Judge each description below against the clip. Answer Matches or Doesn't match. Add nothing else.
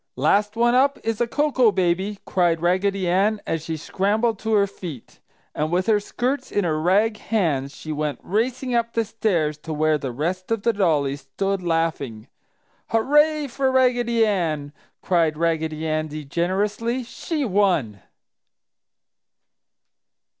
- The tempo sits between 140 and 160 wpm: Matches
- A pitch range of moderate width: Doesn't match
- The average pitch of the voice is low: Doesn't match